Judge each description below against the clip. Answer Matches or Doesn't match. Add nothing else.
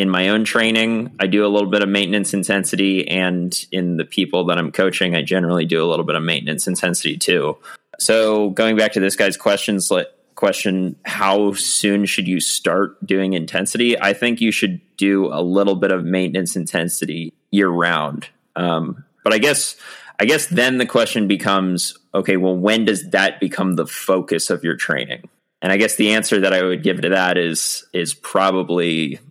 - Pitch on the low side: Matches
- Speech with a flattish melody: Matches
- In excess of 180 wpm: Matches